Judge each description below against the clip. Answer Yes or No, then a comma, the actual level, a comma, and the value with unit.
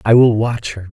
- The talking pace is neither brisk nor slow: No, fast, 255 wpm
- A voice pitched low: Yes, low, 110 Hz